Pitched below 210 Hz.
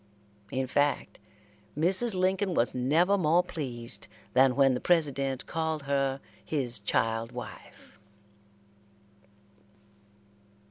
Yes: medium, 140 Hz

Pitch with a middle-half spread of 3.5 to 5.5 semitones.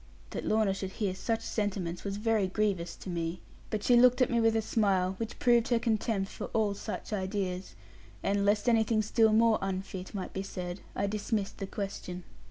No: average, 2.7 semitones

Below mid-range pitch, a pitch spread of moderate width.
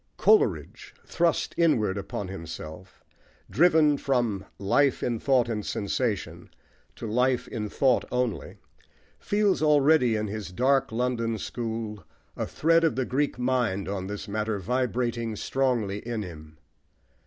Yes: low, 120 Hz; average, 4.4 semitones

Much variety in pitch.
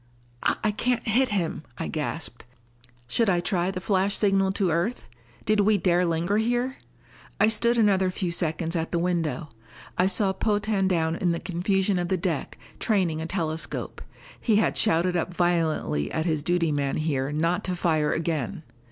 No: average, 3.7 semitones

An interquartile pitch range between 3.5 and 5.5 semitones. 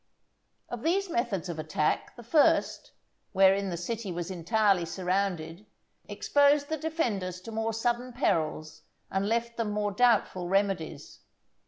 Yes: average, 4.8 semitones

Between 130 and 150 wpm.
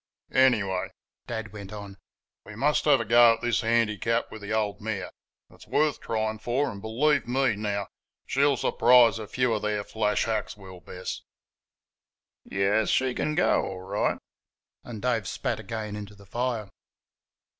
No: average, 160 wpm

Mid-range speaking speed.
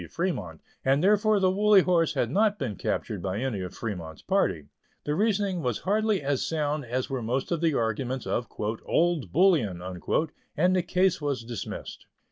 Yes: average, 170 wpm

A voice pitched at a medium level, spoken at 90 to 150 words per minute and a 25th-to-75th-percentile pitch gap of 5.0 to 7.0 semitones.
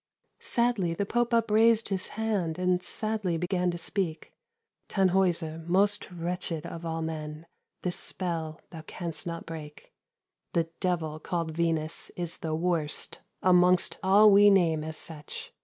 No: medium, 175 Hz; average, 140 wpm; average, 3.0 semitones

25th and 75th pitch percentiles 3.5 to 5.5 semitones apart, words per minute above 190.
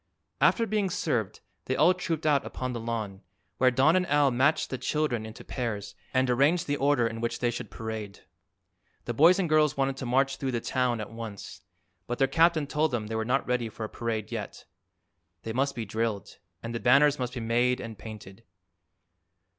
Yes: average, 4.1 semitones; average, 200 wpm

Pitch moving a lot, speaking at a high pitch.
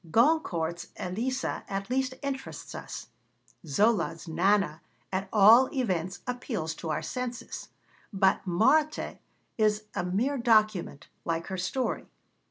Yes: wide, 6.0 semitones; high, 210 Hz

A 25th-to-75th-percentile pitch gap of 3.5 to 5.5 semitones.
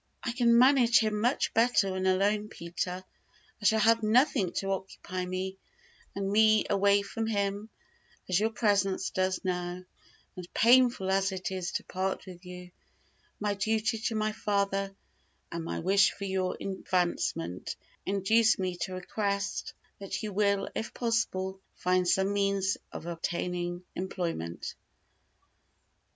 No: narrow, 2.6 semitones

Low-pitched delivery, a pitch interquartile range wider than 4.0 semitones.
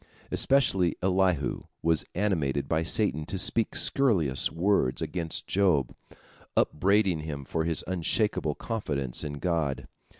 Yes: very low, 85 Hz; average, 4.8 semitones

